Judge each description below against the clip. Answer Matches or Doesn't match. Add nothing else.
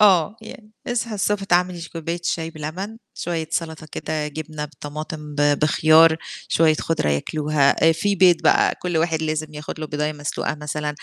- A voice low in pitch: Doesn't match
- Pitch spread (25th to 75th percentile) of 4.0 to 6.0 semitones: Doesn't match